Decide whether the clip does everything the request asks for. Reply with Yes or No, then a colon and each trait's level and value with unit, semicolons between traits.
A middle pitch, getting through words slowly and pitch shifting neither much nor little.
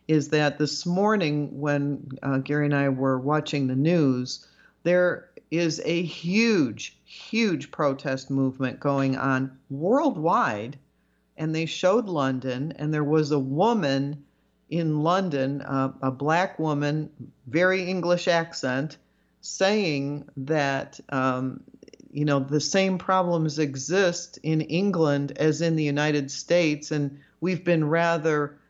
Yes: medium, 150 Hz; slow, 130 wpm; average, 3.4 semitones